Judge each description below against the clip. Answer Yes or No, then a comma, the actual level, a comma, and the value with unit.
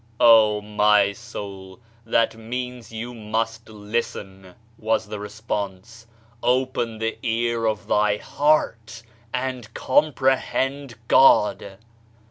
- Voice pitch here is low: Yes, low, 115 Hz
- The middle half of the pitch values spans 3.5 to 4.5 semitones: No, narrow, 2.4 semitones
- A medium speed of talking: No, slow, 100 wpm